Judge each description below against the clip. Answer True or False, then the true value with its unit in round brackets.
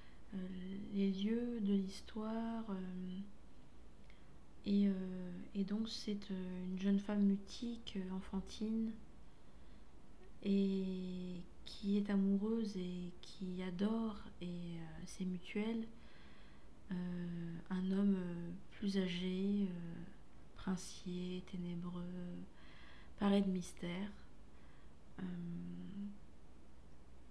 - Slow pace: True (80 wpm)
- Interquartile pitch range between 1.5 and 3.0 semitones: True (2.4 semitones)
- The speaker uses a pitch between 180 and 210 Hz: True (185 Hz)